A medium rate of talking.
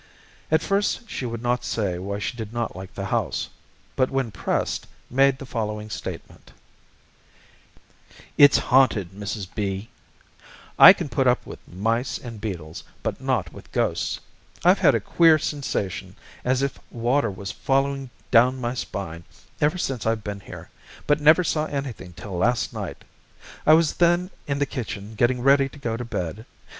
Yes: average, 165 wpm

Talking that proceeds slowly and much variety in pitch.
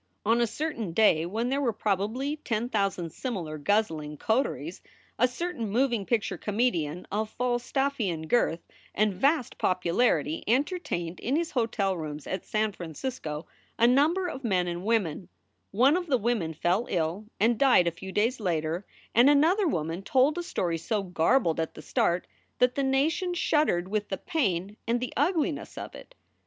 No: average, 165 wpm; wide, 7.0 semitones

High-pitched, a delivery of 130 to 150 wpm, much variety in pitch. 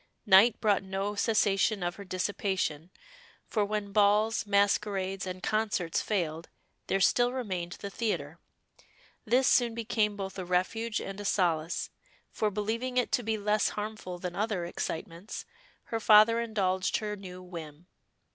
No: high, 200 Hz; average, 145 wpm; average, 2.8 semitones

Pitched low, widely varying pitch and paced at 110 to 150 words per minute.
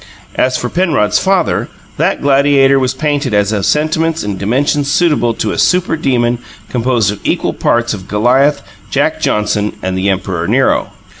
No: low, 125 Hz; wide, 5.7 semitones; average, 160 wpm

